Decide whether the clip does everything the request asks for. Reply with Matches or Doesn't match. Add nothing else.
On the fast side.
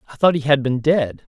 Matches